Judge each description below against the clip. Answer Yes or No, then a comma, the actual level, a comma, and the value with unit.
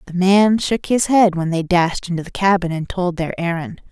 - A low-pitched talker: No, medium, 180 Hz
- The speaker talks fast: Yes, fast, 245 wpm